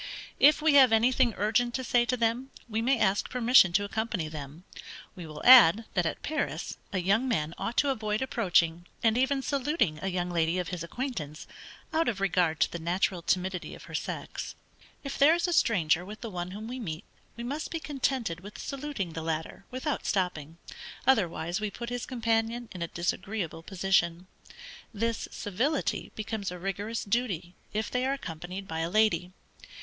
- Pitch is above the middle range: Yes, high, 210 Hz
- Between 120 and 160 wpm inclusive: No, average, 185 wpm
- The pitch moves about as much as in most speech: No, wide, 5.8 semitones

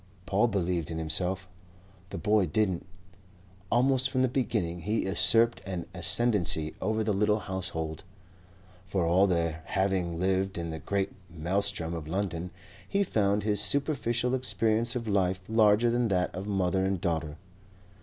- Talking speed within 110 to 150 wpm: Yes, average, 145 wpm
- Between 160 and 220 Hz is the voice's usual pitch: No, very low, 95 Hz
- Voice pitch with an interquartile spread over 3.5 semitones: Yes, average, 4.0 semitones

